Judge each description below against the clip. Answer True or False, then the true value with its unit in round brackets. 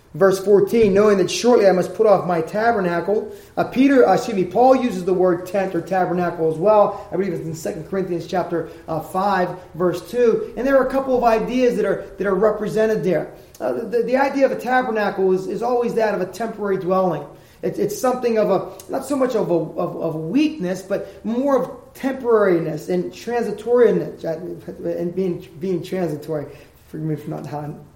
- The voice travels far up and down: False (4.4 semitones)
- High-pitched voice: True (195 Hz)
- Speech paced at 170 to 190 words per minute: False (200 wpm)